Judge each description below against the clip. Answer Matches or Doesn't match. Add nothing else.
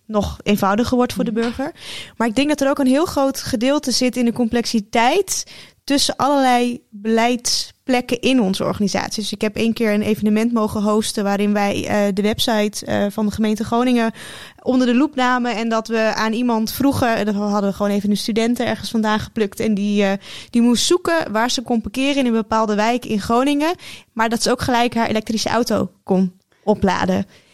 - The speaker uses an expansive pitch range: Doesn't match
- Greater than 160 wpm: Matches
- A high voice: Matches